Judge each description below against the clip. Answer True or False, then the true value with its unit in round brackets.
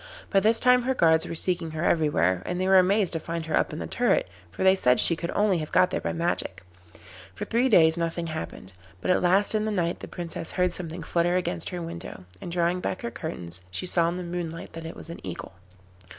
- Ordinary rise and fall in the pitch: False (2.3 semitones)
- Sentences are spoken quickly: True (240 wpm)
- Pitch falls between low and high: True (170 Hz)